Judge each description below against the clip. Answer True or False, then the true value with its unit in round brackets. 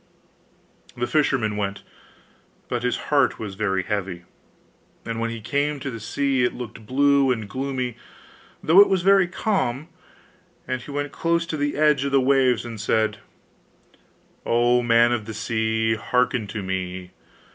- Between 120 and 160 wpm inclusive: True (155 wpm)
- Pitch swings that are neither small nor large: True (4.3 semitones)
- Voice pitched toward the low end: True (120 Hz)